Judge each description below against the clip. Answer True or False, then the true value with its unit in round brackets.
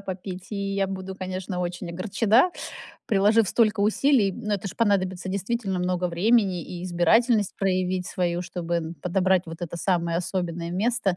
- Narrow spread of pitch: True (2.3 semitones)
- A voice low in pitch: False (185 Hz)